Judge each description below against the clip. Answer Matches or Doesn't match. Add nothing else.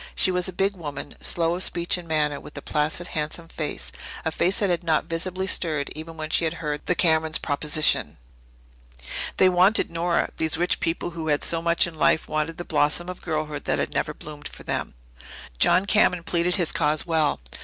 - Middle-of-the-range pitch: Matches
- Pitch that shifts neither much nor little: Doesn't match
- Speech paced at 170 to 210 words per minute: Matches